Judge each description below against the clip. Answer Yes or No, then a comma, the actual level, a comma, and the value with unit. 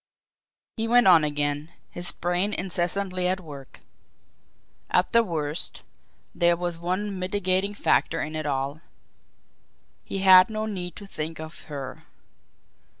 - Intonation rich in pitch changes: No, average, 3.7 semitones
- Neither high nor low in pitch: Yes, medium, 175 Hz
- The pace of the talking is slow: Yes, slow, 130 wpm